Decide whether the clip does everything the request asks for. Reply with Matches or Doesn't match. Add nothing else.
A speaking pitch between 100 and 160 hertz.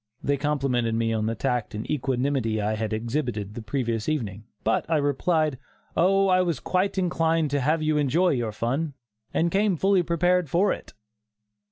Matches